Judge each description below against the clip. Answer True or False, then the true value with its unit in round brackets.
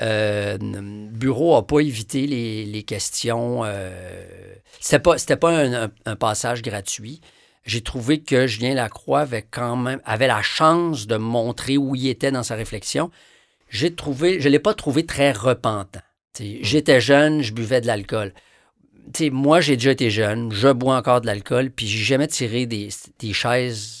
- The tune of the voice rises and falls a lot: False (4.2 semitones)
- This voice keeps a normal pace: True (180 wpm)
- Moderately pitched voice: False (125 Hz)